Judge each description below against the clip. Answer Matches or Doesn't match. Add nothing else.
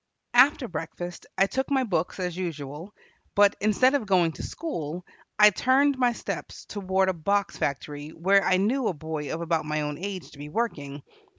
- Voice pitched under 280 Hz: Matches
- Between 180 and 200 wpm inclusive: Matches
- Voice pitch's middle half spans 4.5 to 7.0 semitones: Matches